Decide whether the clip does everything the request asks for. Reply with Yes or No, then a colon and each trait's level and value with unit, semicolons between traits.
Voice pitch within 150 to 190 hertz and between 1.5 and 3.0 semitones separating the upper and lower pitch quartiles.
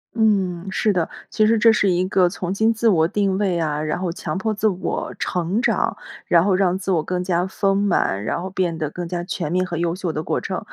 Yes: medium, 185 Hz; narrow, 2.6 semitones